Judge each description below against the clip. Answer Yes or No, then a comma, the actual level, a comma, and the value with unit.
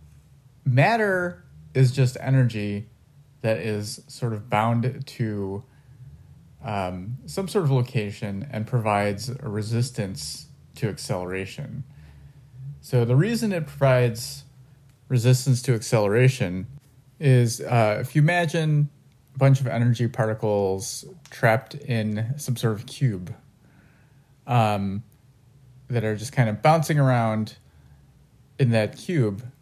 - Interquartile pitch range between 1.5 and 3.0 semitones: No, average, 4.0 semitones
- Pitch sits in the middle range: No, low, 125 Hz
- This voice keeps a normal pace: No, slow, 115 wpm